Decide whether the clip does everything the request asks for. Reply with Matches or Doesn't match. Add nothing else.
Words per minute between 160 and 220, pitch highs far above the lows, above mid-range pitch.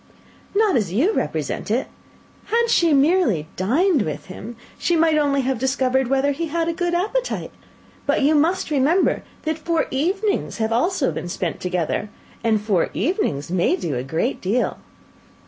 Matches